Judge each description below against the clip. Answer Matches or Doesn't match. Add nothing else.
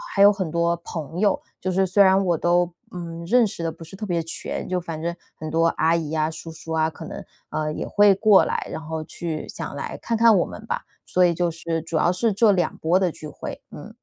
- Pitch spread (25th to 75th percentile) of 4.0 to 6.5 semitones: Doesn't match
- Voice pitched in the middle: Matches